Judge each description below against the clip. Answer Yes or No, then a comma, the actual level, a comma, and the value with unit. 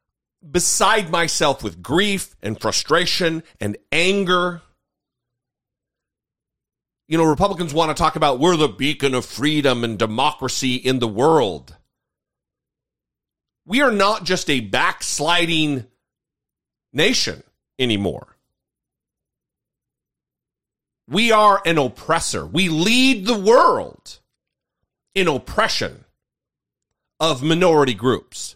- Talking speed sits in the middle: No, slow, 95 wpm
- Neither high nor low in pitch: Yes, medium, 155 Hz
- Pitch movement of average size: No, wide, 5.9 semitones